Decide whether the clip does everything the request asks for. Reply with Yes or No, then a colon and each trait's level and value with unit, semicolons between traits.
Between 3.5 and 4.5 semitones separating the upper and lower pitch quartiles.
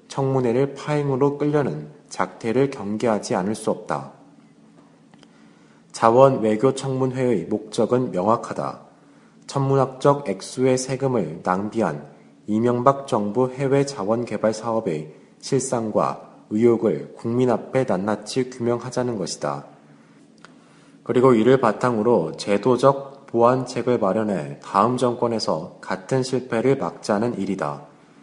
Yes: average, 3.8 semitones